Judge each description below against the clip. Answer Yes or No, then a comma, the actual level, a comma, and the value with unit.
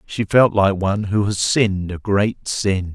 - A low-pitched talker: Yes, low, 100 Hz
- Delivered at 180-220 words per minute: Yes, fast, 205 wpm